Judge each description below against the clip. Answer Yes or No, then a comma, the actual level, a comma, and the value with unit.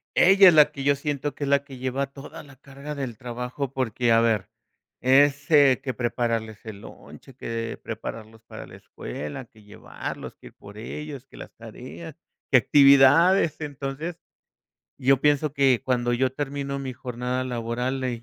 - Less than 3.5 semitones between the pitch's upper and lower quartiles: Yes, average, 2.9 semitones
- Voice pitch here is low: Yes, low, 130 Hz